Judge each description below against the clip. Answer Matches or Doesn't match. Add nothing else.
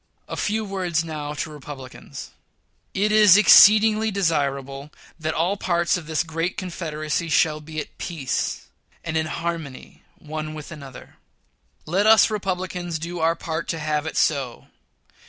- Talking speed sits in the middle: Matches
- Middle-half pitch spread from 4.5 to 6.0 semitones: Doesn't match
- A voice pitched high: Doesn't match